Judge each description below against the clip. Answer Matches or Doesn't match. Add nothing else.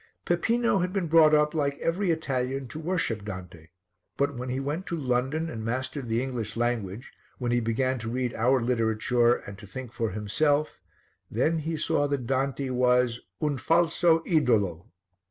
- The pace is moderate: Matches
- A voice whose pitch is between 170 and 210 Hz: Doesn't match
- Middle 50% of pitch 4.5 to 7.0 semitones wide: Matches